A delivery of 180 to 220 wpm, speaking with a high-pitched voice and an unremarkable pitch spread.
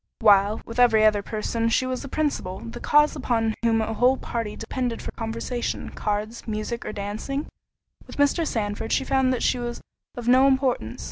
Yes: average, 185 wpm; high, 230 Hz; average, 3.1 semitones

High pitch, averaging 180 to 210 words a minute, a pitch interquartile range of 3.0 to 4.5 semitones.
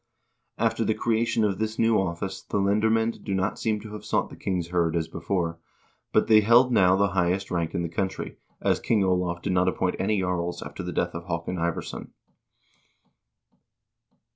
No: very low, 95 Hz; average, 185 wpm; average, 3.5 semitones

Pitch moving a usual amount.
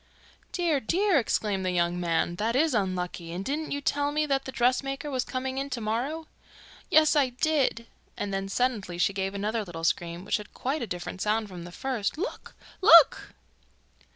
No: wide, 6.8 semitones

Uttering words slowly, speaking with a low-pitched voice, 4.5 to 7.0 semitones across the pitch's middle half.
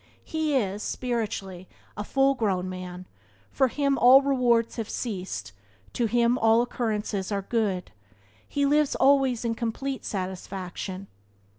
No: slow, 130 wpm; high, 230 Hz; average, 5.2 semitones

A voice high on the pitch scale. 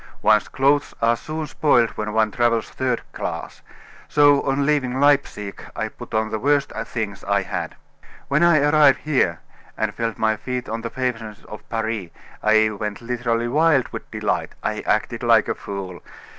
No: low, 115 Hz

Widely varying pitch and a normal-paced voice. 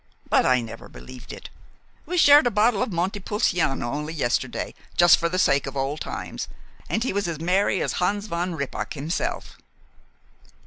Yes: wide, 6.4 semitones; average, 175 wpm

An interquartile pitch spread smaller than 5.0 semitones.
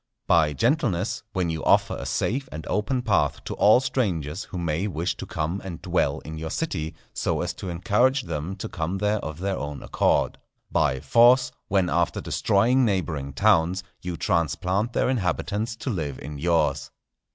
No: average, 5.3 semitones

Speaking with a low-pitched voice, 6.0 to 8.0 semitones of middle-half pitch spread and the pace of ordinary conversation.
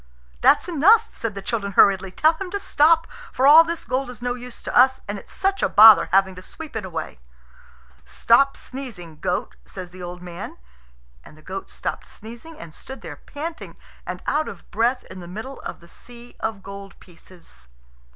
No: high, 225 Hz; wide, 6.8 semitones; average, 190 wpm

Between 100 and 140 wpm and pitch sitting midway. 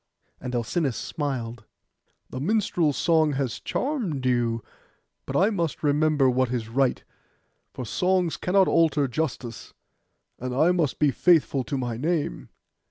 Yes: slow, 135 wpm; medium, 145 Hz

